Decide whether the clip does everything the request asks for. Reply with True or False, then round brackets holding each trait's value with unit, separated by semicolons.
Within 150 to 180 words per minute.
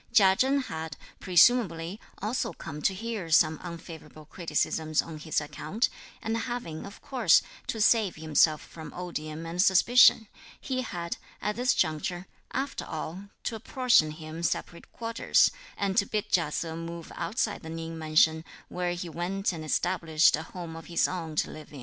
True (165 wpm)